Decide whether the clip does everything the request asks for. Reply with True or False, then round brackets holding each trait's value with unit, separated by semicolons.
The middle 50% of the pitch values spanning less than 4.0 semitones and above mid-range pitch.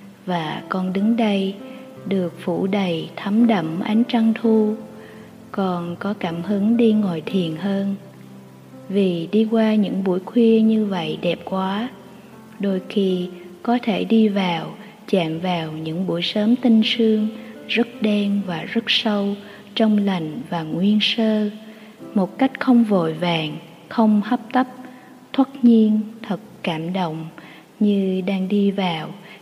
True (3.5 semitones; 205 Hz)